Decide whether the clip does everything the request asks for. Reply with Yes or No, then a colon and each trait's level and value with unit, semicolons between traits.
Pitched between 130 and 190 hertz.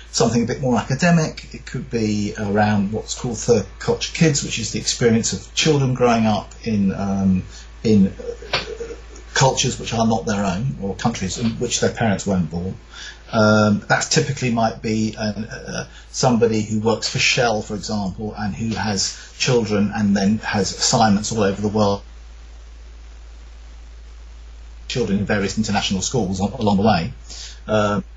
No: low, 105 Hz